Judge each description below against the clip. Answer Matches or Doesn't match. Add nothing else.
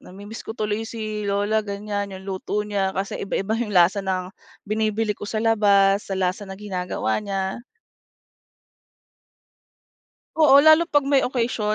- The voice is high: Matches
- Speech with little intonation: Matches